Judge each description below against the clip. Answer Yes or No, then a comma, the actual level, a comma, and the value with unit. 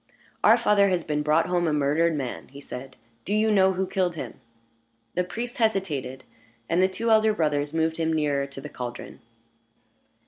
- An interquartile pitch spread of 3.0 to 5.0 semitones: Yes, average, 4.7 semitones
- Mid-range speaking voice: Yes, medium, 165 Hz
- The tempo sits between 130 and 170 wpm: No, average, 180 wpm